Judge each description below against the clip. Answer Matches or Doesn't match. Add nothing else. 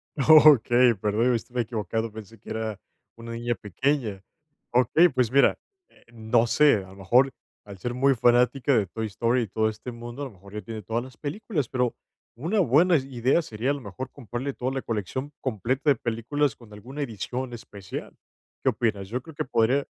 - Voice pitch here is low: Matches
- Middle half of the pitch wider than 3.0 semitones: Matches